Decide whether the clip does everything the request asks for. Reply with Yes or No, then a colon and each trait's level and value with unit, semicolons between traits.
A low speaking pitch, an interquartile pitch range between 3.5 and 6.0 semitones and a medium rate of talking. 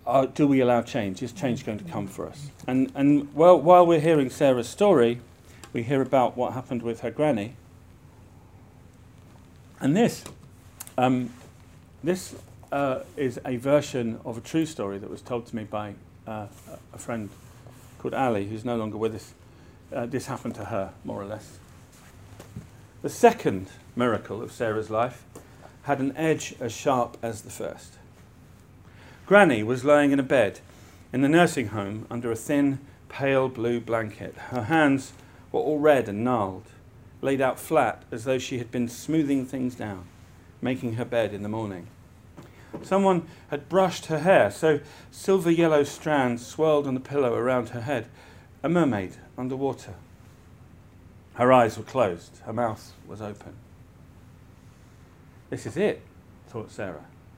Yes: low, 120 Hz; average, 4.6 semitones; average, 155 wpm